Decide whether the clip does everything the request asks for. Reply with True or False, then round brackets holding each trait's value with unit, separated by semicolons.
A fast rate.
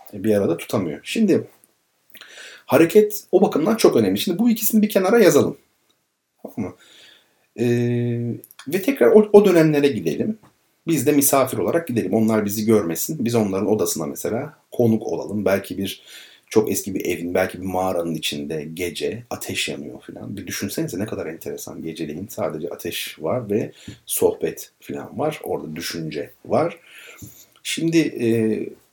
True (145 wpm)